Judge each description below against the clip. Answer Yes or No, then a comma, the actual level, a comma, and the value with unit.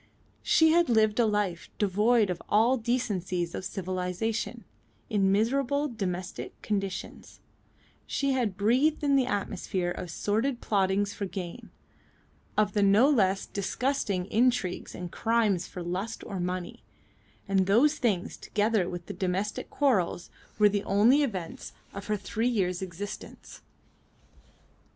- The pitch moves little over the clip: No, average, 4.1 semitones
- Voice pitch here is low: No, high, 205 Hz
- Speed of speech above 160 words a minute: No, slow, 135 wpm